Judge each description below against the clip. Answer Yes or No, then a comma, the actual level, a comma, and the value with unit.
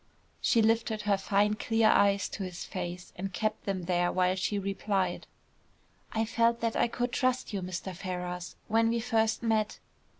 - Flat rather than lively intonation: No, average, 3.4 semitones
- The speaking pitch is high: Yes, high, 205 Hz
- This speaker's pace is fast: No, average, 170 wpm